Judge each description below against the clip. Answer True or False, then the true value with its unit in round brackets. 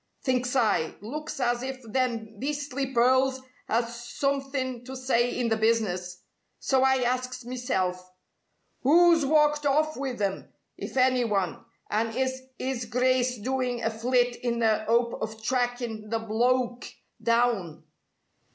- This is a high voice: True (245 Hz)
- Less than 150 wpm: True (135 wpm)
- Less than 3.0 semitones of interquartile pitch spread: True (2.6 semitones)